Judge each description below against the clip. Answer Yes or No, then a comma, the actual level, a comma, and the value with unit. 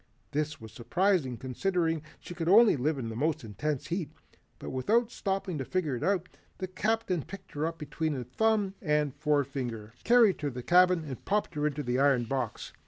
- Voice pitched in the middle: Yes, medium, 155 Hz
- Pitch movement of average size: No, wide, 5.7 semitones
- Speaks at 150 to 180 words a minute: No, average, 190 wpm